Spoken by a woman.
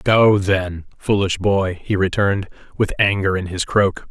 No: male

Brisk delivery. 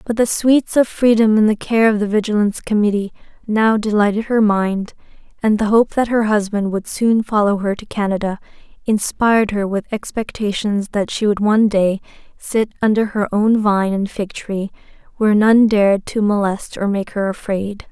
No: average, 180 wpm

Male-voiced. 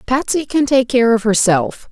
No: female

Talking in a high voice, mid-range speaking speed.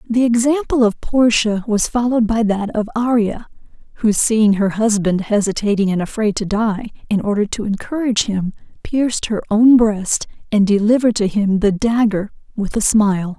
Yes: high, 215 Hz; average, 165 wpm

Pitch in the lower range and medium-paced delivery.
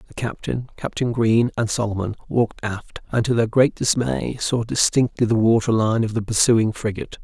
Yes: low, 115 Hz; average, 180 wpm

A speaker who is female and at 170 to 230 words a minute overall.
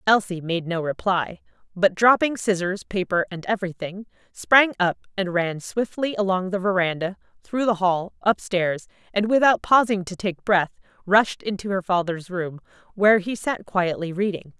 No: female; average, 155 wpm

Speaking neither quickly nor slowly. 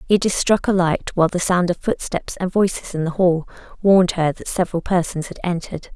No: fast, 210 wpm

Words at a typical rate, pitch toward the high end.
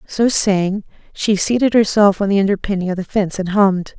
Yes: average, 195 wpm; high, 200 Hz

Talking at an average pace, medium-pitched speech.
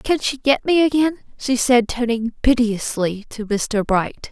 No: average, 165 wpm; high, 240 Hz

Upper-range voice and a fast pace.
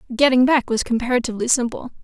No: high, 245 Hz; average, 145 wpm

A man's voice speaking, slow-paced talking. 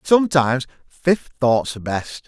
Yes: male; slow, 130 wpm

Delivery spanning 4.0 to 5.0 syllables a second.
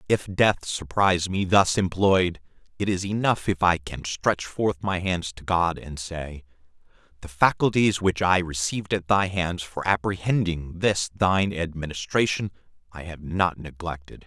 Yes: 4.4 syllables/s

